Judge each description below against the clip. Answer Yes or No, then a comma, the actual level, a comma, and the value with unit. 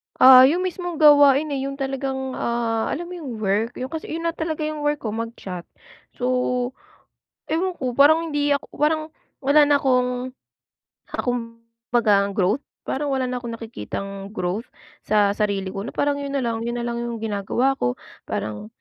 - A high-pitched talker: Yes, very high, 250 Hz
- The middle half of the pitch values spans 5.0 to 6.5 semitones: No, average, 4.3 semitones